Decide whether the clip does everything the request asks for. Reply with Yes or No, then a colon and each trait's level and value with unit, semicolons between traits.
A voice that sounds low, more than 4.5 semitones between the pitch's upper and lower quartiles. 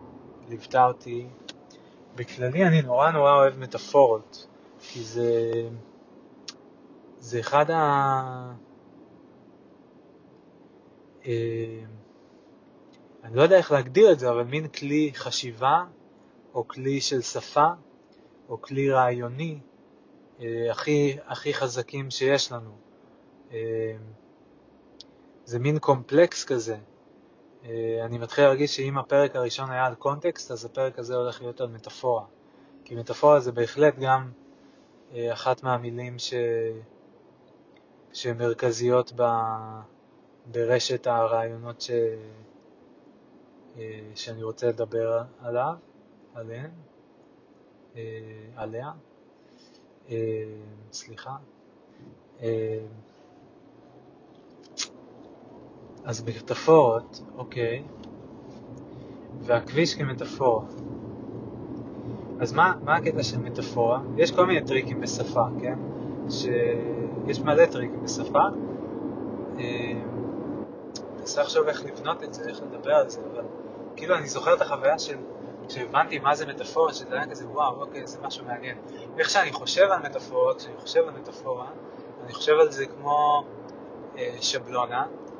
No: low, 125 Hz; average, 3.6 semitones